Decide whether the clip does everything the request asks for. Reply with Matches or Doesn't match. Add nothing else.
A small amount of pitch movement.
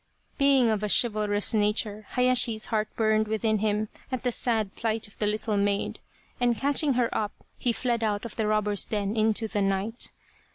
Matches